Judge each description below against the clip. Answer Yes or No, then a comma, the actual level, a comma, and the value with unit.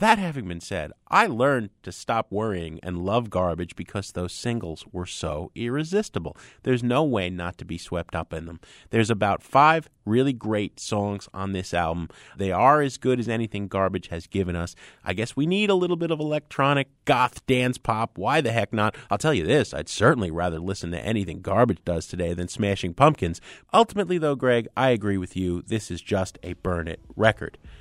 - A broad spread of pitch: Yes, wide, 6.2 semitones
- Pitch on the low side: Yes, low, 100 Hz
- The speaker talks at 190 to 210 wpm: Yes, average, 200 wpm